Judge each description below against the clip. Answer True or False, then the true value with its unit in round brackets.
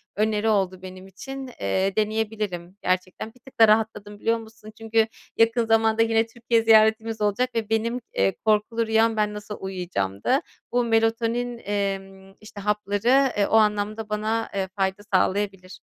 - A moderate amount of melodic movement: False (2.3 semitones)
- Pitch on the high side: True (215 Hz)